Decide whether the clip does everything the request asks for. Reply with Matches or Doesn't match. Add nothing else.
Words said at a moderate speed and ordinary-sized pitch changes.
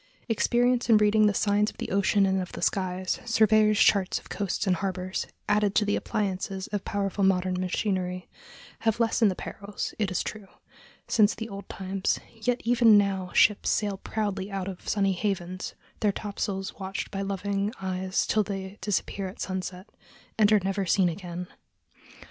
Doesn't match